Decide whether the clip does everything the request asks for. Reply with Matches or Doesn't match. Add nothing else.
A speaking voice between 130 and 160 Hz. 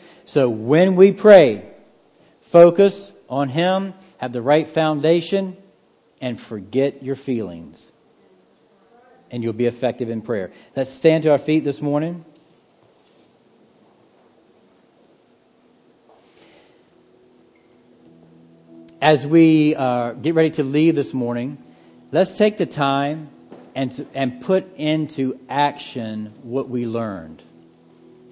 Matches